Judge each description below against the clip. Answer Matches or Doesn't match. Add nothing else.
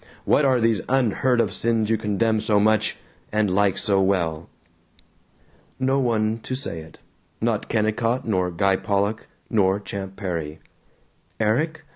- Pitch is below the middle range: Matches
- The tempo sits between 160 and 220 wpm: Doesn't match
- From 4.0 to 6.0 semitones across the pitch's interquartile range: Doesn't match